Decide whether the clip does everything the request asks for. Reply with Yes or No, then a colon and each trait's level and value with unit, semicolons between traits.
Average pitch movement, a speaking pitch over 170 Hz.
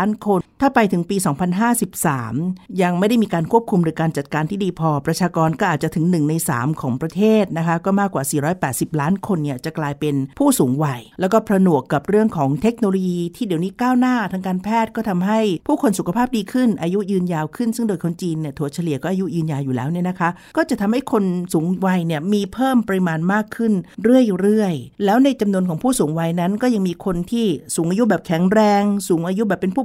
Yes: average, 4.7 semitones; medium, 185 Hz